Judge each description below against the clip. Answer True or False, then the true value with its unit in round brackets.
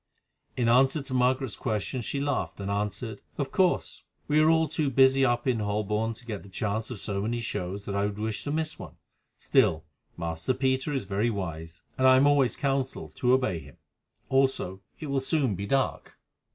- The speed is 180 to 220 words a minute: True (195 wpm)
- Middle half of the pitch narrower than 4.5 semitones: False (4.9 semitones)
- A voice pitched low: True (120 Hz)